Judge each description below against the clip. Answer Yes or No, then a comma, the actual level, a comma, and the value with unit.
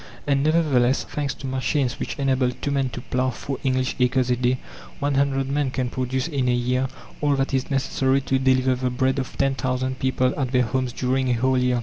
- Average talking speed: No, fast, 210 wpm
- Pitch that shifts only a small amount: Yes, narrow, 1.3 semitones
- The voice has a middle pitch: No, low, 130 Hz